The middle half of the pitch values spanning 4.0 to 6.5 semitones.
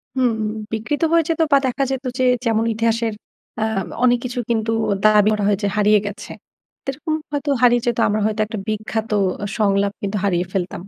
No: average, 2.9 semitones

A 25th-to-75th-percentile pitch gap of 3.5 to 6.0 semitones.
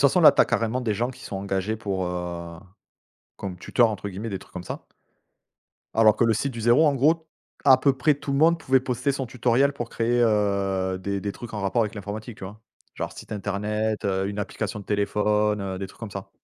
Yes: average, 3.8 semitones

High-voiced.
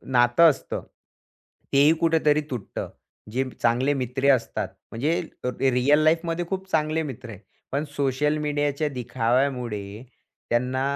No: low, 135 Hz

